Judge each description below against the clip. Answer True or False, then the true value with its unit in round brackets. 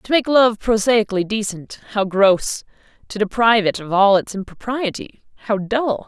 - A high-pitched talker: True (215 Hz)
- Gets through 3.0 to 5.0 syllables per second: True (4.7 syllables/s)